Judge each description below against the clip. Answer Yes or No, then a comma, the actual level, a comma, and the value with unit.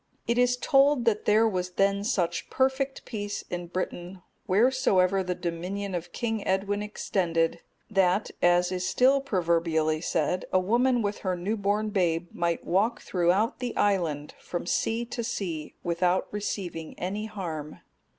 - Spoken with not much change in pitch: No, average, 3.7 semitones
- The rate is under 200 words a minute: Yes, average, 150 wpm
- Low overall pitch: No, high, 190 Hz